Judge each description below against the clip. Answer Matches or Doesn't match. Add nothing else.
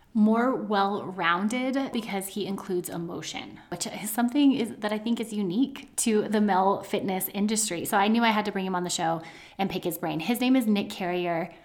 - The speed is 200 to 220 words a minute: Matches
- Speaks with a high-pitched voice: Matches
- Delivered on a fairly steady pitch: Doesn't match